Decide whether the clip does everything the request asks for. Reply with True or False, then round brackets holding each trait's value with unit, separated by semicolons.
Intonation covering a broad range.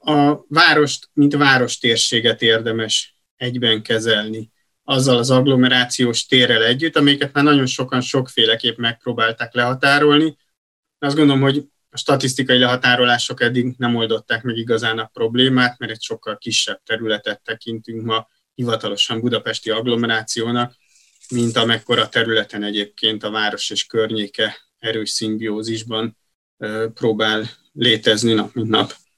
False (2.5 semitones)